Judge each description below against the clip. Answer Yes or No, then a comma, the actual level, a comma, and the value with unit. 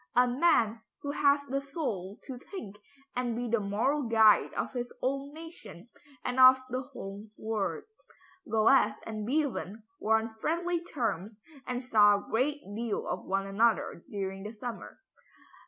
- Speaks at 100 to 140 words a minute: No, average, 155 wpm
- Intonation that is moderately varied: Yes, average, 4.5 semitones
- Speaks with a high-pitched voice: Yes, high, 235 Hz